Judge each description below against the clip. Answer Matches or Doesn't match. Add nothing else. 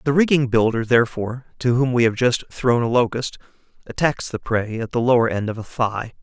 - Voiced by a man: Matches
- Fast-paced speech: Matches